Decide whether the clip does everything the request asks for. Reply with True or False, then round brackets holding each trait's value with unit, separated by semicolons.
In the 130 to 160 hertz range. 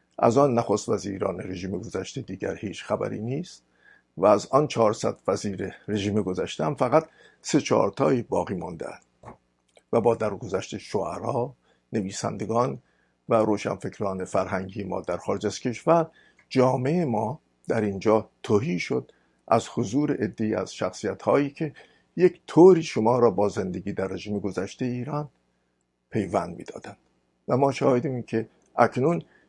False (105 Hz)